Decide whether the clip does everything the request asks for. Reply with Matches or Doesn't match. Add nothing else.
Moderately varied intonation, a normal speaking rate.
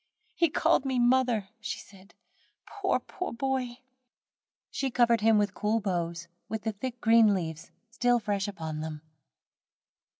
Matches